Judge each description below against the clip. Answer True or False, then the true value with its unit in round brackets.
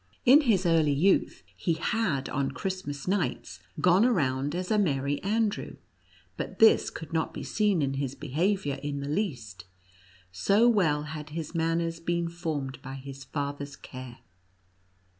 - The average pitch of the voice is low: False (160 Hz)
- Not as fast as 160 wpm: True (150 wpm)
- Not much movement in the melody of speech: False (5.1 semitones)